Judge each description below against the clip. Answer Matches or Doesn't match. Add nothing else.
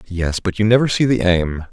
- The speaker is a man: Matches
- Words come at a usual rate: Doesn't match